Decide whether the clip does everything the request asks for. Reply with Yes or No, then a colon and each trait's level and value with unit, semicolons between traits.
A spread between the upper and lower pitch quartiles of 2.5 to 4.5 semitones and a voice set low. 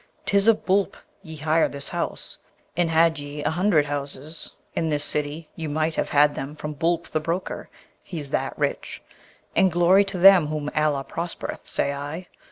No: average, 2.9 semitones; medium, 160 Hz